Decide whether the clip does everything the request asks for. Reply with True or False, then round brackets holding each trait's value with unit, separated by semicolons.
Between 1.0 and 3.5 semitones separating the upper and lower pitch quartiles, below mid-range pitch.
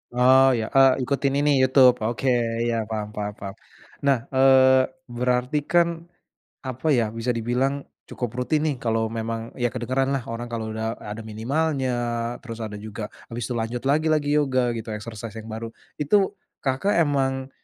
True (3.1 semitones; 125 Hz)